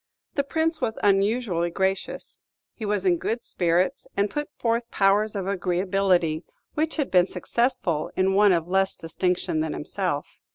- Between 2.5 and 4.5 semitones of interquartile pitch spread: Yes, average, 3.8 semitones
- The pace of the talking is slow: No, average, 155 wpm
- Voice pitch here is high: Yes, high, 195 Hz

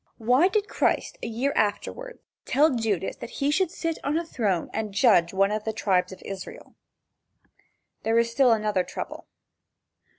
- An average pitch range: No, wide, 5.7 semitones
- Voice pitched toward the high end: Yes, high, 225 Hz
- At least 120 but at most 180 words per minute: Yes, average, 165 wpm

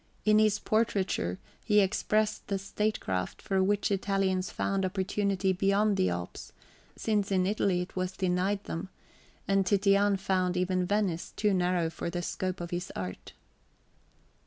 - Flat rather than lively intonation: Yes, narrow, 2.1 semitones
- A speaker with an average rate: Yes, average, 145 wpm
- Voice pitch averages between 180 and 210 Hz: Yes, high, 190 Hz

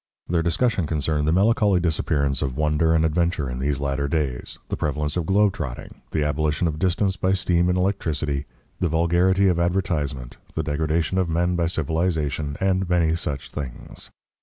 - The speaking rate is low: No, average, 170 wpm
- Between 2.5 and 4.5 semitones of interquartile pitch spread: Yes, average, 3.4 semitones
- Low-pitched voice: Yes, very low, 80 Hz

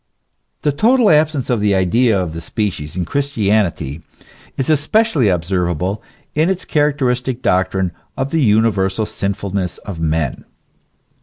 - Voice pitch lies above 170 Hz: No, low, 105 Hz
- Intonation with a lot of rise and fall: Yes, wide, 7.4 semitones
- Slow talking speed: Yes, slow, 130 wpm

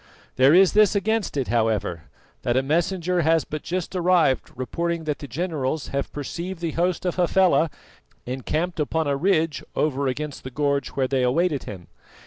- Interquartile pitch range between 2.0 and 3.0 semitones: No, average, 4.8 semitones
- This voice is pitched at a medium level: Yes, medium, 155 Hz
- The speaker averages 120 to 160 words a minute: No, average, 170 wpm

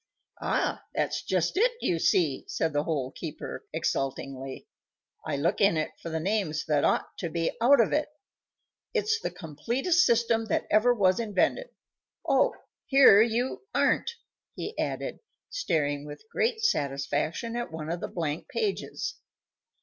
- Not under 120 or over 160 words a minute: Yes, average, 150 wpm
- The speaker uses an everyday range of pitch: No, wide, 8.1 semitones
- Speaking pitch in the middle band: Yes, medium, 180 Hz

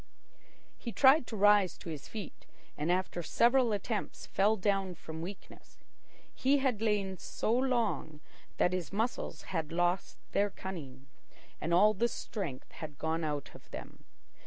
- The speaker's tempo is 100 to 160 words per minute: Yes, average, 150 wpm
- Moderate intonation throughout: Yes, average, 4.9 semitones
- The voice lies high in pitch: Yes, high, 195 Hz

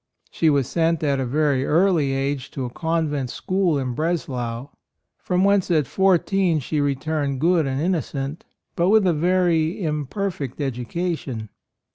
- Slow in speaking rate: No, average, 175 wpm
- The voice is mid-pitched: Yes, medium, 155 Hz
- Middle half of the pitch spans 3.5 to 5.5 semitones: Yes, average, 4.5 semitones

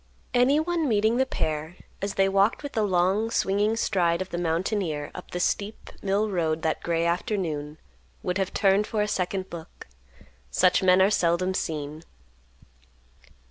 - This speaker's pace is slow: No, average, 155 wpm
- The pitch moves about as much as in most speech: Yes, average, 3.6 semitones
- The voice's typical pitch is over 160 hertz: Yes, high, 190 Hz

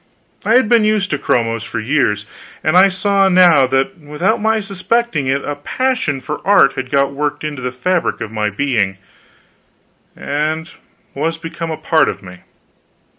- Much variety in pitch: Yes, wide, 6.3 semitones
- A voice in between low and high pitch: Yes, medium, 155 Hz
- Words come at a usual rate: Yes, average, 170 wpm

